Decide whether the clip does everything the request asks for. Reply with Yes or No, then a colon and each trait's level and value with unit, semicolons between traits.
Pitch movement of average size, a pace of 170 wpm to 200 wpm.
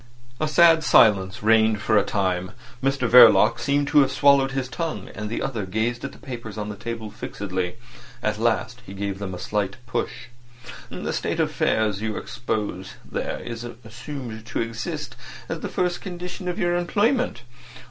Yes: average, 4.8 semitones; average, 175 wpm